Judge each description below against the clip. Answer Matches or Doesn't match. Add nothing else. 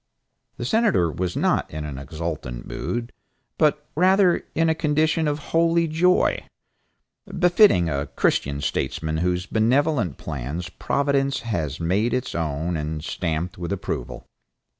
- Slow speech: Matches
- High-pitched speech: Doesn't match